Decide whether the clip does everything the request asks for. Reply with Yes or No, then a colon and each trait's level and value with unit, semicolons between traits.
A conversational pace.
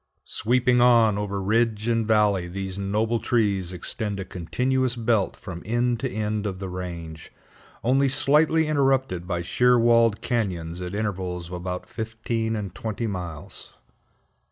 Yes: average, 145 wpm